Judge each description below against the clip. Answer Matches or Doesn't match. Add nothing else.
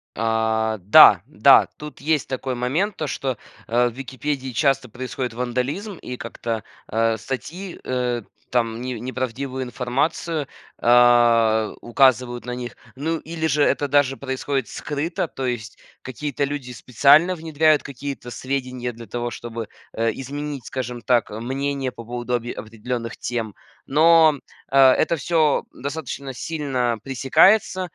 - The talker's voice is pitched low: Matches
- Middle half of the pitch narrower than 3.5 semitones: Matches